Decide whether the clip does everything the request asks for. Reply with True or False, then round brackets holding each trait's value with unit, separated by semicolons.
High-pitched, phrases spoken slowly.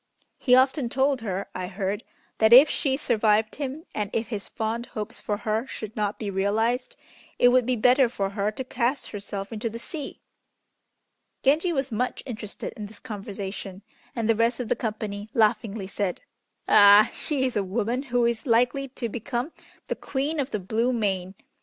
False (225 Hz; 180 wpm)